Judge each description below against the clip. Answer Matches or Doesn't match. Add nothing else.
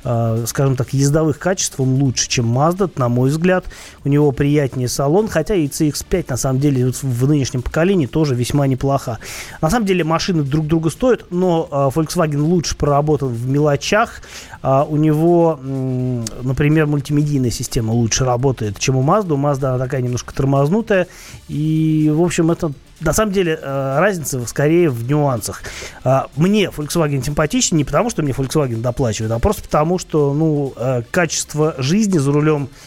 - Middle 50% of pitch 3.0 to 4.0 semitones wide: Matches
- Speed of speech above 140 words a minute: Matches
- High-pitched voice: Doesn't match